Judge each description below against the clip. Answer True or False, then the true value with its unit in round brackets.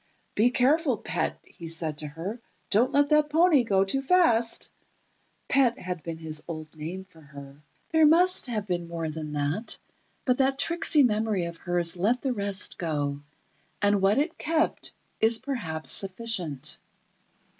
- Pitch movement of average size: False (8.2 semitones)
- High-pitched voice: True (200 Hz)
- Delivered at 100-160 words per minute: True (155 wpm)